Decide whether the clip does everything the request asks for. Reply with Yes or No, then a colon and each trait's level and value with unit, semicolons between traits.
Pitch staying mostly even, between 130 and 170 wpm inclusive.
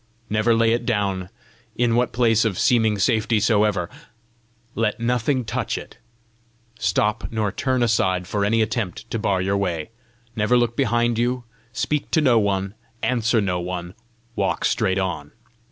No: average, 3.2 semitones; average, 155 wpm